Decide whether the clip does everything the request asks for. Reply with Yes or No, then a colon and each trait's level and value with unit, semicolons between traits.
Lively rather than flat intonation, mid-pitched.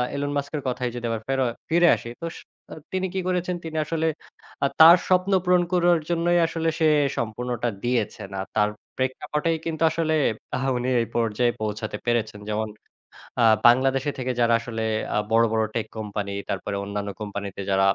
No: wide, 6.8 semitones; low, 125 Hz